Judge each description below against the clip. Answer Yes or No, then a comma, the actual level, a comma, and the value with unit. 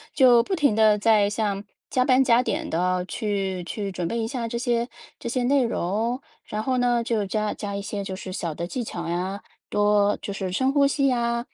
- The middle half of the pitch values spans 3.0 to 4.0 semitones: Yes, average, 3.7 semitones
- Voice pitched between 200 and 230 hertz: Yes, high, 220 Hz